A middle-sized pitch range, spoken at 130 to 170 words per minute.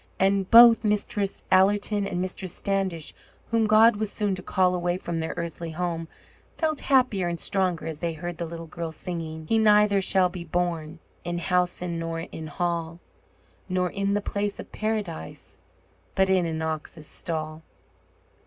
Yes: average, 3.3 semitones; average, 160 wpm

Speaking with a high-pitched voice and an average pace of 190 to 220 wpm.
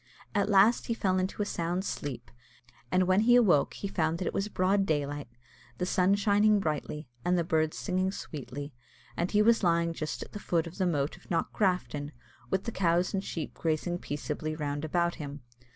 No: medium, 175 Hz; average, 200 wpm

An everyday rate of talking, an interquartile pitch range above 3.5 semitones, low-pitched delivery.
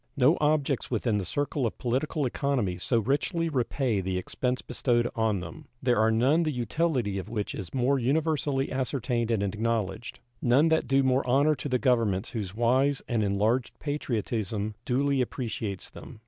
Yes: average, 165 wpm; average, 4.1 semitones; low, 125 Hz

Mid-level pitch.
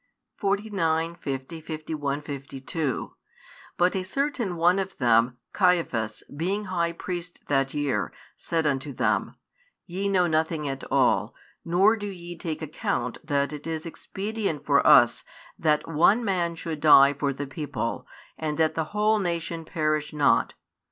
Yes: medium, 160 Hz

